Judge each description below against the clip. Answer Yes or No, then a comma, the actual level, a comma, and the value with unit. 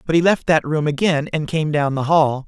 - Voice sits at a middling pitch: Yes, medium, 155 Hz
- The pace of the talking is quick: Yes, fast, 265 wpm